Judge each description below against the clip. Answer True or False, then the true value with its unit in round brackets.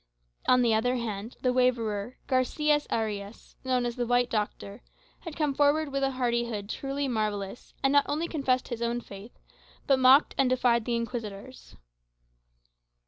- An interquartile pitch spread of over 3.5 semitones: False (3.2 semitones)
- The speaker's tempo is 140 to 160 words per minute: True (155 wpm)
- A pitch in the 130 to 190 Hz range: False (245 Hz)